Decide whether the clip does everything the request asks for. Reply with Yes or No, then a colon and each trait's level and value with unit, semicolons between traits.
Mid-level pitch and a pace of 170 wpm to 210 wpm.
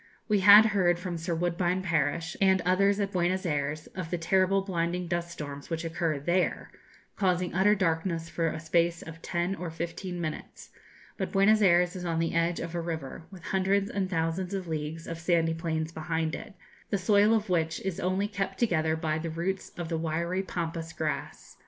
Yes: medium, 170 Hz; average, 190 wpm